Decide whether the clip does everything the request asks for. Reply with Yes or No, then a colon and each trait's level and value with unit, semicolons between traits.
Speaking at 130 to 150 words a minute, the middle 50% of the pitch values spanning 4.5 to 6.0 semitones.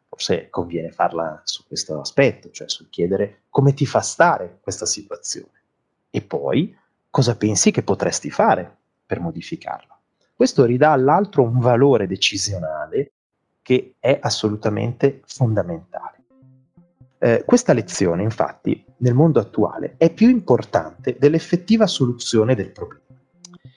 No: average, 120 wpm; average, 5.1 semitones